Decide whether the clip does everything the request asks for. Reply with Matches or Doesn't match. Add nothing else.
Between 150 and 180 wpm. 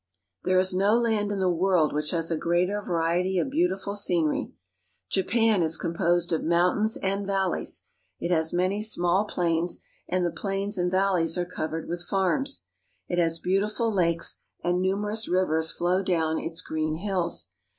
Matches